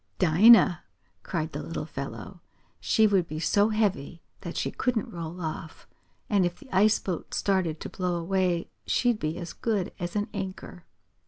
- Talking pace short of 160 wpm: No, average, 165 wpm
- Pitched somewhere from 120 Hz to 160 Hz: No, medium, 185 Hz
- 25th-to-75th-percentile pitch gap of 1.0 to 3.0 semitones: No, average, 3.5 semitones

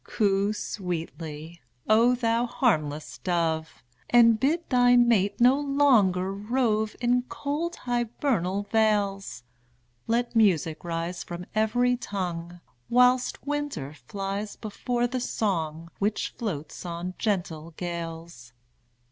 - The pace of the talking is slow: Yes, slow, 105 wpm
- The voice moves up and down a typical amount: No, wide, 6.1 semitones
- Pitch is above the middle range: Yes, high, 205 Hz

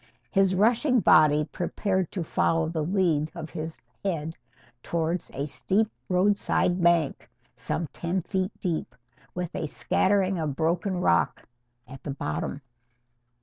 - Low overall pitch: No, medium, 170 Hz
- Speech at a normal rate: No, slow, 130 wpm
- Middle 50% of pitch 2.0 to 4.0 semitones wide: Yes, average, 3.4 semitones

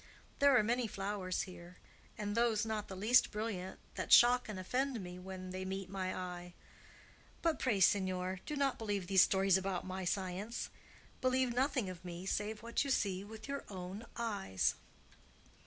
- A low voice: No, high, 195 Hz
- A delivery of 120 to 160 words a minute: No, average, 170 wpm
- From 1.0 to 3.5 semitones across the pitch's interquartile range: No, average, 3.9 semitones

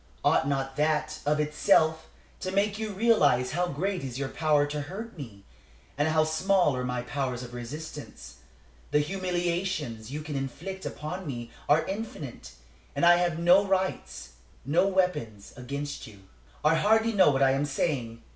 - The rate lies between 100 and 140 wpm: No, average, 165 wpm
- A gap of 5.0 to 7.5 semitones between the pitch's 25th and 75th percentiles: Yes, wide, 5.4 semitones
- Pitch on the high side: No, medium, 150 Hz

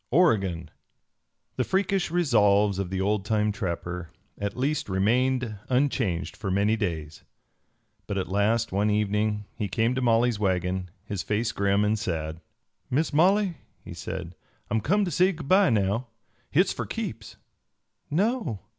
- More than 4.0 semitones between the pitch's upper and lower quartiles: Yes, average, 5.1 semitones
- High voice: No, low, 105 Hz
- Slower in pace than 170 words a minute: Yes, average, 145 wpm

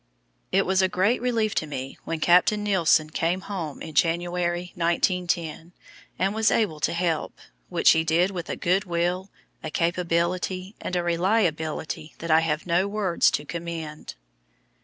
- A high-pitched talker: No, medium, 175 Hz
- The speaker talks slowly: No, average, 160 wpm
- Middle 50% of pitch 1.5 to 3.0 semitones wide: Yes, narrow, 2.4 semitones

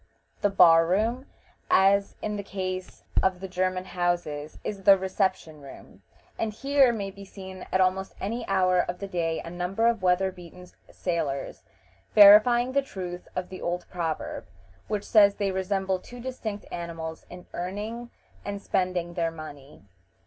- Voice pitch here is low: No, high, 190 Hz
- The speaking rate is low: No, average, 155 wpm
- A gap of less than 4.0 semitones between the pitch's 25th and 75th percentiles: Yes, narrow, 2.5 semitones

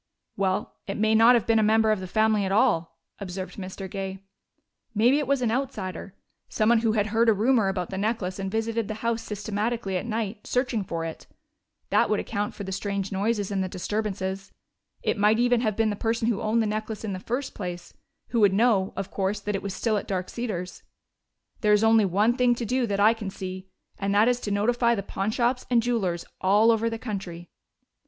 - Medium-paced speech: No, fast, 215 wpm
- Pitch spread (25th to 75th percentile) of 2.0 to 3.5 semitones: Yes, average, 2.9 semitones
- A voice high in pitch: Yes, high, 210 Hz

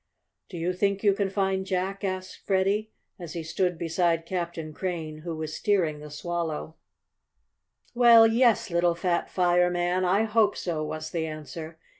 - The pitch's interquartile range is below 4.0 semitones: Yes, average, 3.0 semitones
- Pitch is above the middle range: No, medium, 180 Hz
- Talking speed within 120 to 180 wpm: Yes, average, 155 wpm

